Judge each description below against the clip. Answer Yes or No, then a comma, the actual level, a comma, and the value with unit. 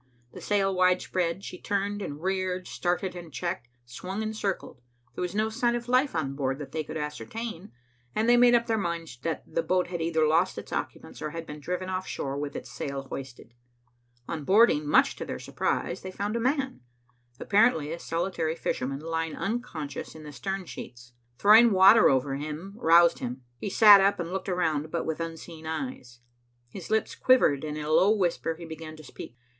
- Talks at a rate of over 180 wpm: Yes, average, 195 wpm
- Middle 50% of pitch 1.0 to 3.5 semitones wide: No, average, 4.5 semitones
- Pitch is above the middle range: No, medium, 170 Hz